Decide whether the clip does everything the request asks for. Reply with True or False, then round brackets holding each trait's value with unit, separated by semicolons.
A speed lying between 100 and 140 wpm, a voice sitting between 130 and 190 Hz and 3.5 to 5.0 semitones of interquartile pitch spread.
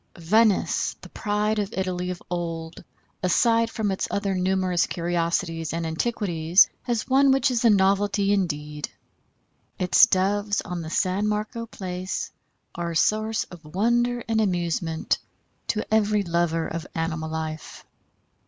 True (135 wpm; 185 Hz; 4.1 semitones)